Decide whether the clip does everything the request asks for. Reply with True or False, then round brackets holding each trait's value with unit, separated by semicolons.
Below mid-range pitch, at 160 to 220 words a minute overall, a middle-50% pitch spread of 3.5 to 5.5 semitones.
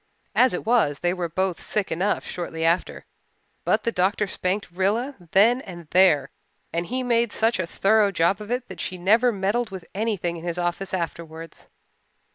False (190 Hz; 180 wpm; 4.2 semitones)